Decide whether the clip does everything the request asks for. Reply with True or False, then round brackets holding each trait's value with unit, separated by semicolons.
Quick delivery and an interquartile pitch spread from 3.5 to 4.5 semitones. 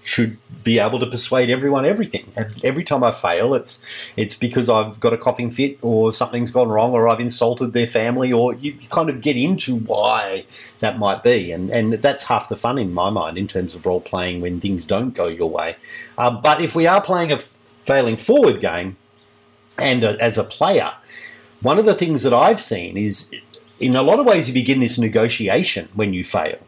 True (210 wpm; 3.9 semitones)